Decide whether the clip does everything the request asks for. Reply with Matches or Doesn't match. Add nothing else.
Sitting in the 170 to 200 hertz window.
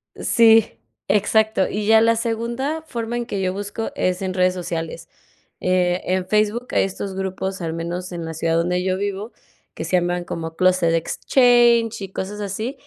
Matches